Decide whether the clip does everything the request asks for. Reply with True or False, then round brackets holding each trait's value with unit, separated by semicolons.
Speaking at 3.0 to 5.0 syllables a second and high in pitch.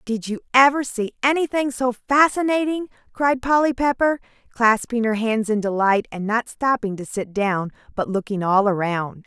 True (4.8 syllables/s; 235 Hz)